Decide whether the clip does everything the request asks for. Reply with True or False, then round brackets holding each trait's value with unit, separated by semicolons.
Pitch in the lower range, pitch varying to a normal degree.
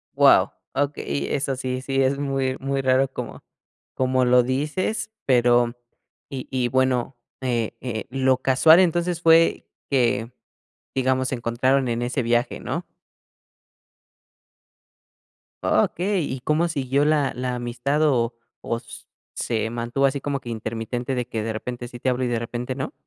False (130 Hz; 2.2 semitones)